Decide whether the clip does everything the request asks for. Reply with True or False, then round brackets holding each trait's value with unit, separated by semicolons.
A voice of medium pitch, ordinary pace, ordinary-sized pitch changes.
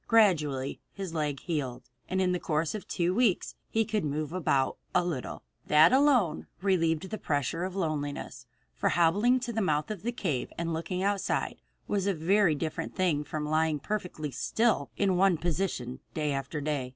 True (170 Hz; 175 wpm; 4.5 semitones)